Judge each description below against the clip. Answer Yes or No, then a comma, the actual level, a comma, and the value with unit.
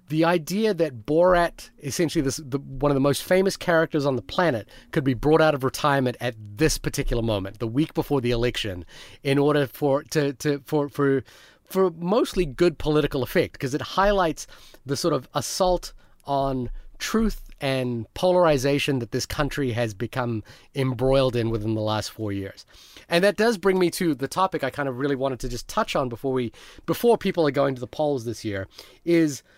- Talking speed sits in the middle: Yes, average, 195 wpm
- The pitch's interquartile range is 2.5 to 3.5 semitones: No, average, 4.5 semitones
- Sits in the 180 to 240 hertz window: No, medium, 140 Hz